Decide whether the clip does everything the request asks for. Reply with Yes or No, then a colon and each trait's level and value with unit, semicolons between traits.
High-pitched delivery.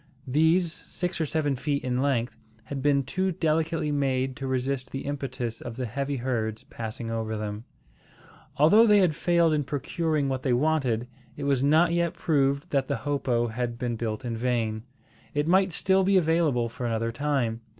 No: low, 135 Hz